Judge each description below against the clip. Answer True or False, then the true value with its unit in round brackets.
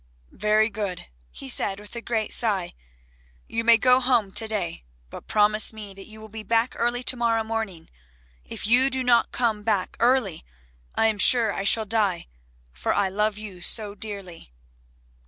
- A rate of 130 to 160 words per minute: False (175 wpm)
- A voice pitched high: True (215 Hz)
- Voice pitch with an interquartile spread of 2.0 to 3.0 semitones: True (2.5 semitones)